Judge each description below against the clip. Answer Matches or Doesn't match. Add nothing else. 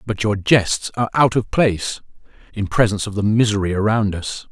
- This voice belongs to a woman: Doesn't match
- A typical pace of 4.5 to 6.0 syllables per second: Matches